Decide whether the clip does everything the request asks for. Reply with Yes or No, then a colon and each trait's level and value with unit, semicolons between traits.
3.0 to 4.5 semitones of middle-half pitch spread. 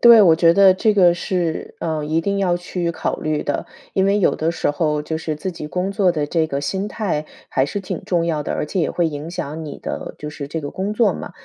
Yes: average, 3.7 semitones